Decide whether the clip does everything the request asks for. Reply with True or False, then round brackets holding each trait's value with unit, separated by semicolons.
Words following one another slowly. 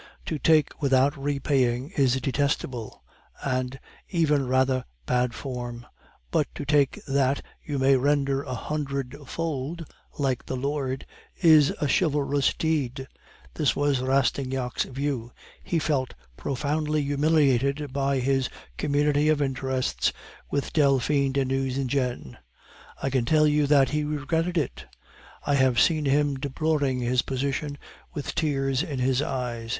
True (130 wpm)